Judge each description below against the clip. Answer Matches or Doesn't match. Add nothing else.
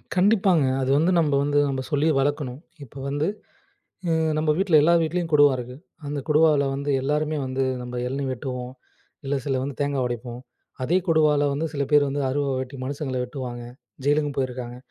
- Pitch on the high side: Doesn't match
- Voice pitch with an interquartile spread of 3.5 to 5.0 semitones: Doesn't match